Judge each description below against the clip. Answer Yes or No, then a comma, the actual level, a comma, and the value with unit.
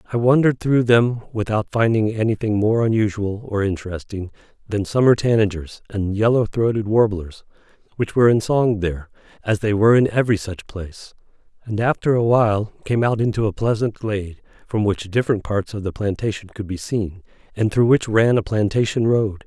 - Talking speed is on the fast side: No, average, 175 wpm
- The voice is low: Yes, low, 110 Hz